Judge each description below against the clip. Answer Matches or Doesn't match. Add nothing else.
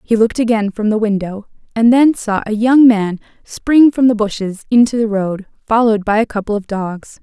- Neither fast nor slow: Doesn't match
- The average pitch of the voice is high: Matches